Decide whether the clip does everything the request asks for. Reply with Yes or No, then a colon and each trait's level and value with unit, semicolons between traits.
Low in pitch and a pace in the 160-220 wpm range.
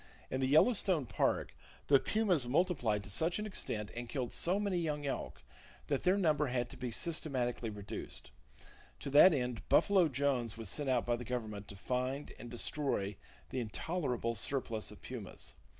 Yes: low, 130 Hz; average, 170 wpm